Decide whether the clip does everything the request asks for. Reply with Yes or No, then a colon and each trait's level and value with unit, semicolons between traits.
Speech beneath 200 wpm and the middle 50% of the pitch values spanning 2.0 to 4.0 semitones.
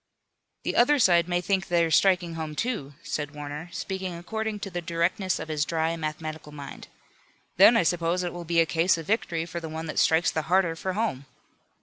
No: fast, 205 wpm; average, 2.8 semitones